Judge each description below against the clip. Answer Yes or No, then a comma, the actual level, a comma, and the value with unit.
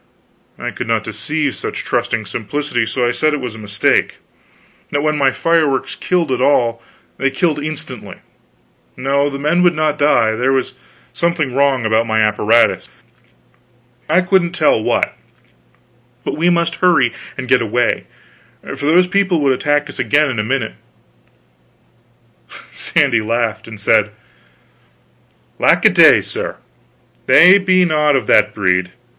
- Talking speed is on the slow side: No, average, 150 wpm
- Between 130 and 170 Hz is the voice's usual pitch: Yes, medium, 140 Hz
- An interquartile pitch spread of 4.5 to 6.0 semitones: Yes, average, 5.1 semitones